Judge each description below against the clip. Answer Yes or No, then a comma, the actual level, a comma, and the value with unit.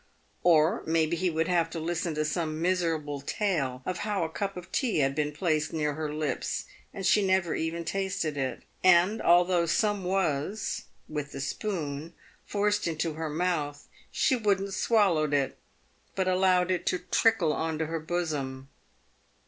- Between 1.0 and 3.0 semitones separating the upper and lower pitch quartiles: No, average, 3.4 semitones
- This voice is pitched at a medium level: Yes, medium, 170 Hz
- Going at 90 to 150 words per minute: No, average, 165 wpm